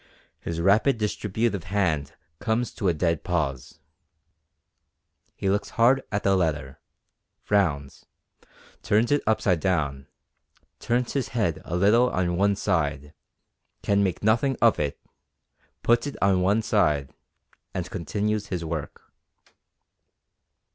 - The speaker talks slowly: Yes, slow, 120 wpm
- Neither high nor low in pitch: No, very low, 95 Hz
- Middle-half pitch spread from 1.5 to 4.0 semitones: No, average, 4.8 semitones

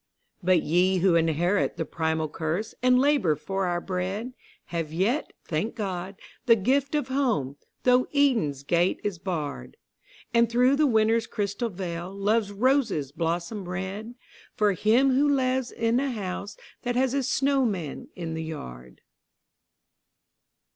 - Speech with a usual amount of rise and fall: No, wide, 6.6 semitones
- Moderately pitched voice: No, high, 200 Hz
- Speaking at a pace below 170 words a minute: Yes, average, 140 wpm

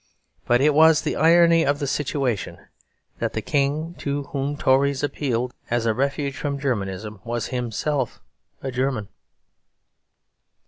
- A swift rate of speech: No, slow, 135 wpm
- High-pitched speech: No, medium, 140 Hz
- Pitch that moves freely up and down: No, average, 3.2 semitones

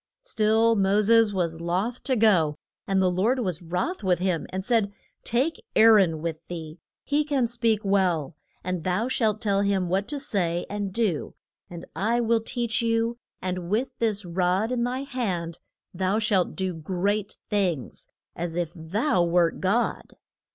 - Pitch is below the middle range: No, high, 200 Hz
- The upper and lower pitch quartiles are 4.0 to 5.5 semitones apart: Yes, average, 4.4 semitones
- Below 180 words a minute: Yes, average, 165 wpm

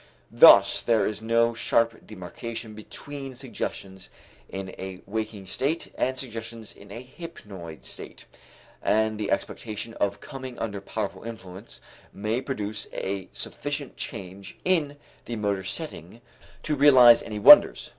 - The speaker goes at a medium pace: No, slow, 130 wpm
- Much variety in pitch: No, average, 3.9 semitones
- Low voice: Yes, low, 110 Hz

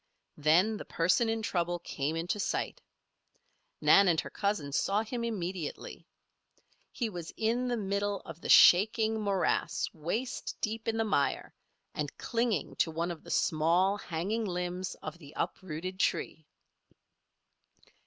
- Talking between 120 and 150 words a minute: Yes, average, 140 wpm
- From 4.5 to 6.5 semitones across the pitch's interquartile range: Yes, average, 4.8 semitones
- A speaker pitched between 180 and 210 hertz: Yes, medium, 185 Hz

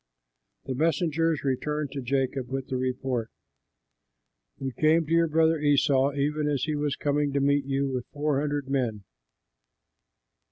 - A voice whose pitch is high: No, medium, 140 Hz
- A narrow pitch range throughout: Yes, narrow, 2.2 semitones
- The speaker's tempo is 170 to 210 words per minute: No, average, 155 wpm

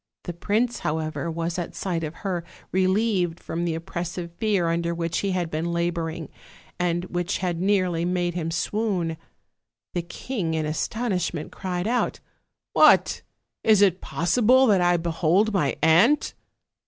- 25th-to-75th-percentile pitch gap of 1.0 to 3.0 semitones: Yes, average, 2.7 semitones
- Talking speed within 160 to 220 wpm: No, average, 150 wpm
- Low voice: No, medium, 175 Hz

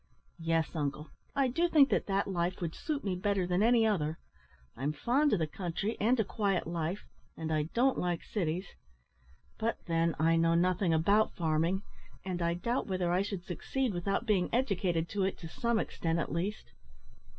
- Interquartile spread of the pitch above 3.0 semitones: Yes, average, 4.3 semitones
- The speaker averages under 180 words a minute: No, average, 185 wpm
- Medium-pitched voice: Yes, medium, 180 Hz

